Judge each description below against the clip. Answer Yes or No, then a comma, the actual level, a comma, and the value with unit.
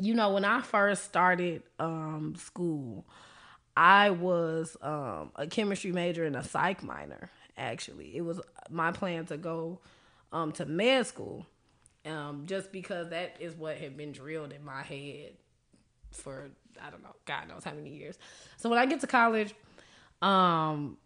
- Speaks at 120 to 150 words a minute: No, average, 160 wpm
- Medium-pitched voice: Yes, medium, 170 Hz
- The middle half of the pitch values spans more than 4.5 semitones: No, average, 4.2 semitones